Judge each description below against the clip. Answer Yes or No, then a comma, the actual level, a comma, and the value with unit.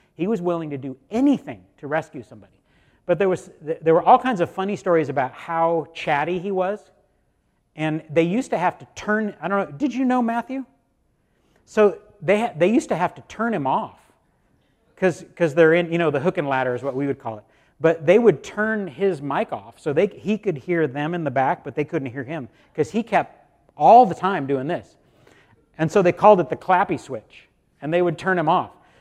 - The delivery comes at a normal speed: No, fast, 220 wpm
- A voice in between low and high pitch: Yes, medium, 175 Hz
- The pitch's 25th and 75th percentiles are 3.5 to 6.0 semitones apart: Yes, average, 4.7 semitones